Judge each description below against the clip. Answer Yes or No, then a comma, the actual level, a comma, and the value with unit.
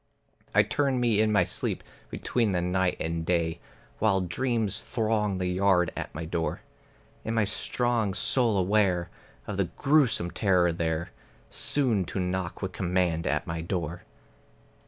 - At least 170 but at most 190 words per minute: No, average, 150 wpm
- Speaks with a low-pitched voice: Yes, very low, 95 Hz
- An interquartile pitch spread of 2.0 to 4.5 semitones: Yes, average, 3.9 semitones